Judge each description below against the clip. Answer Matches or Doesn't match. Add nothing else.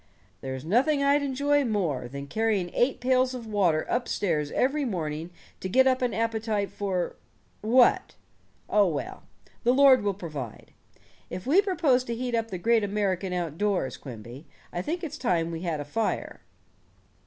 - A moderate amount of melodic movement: Doesn't match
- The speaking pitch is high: Matches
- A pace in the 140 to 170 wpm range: Matches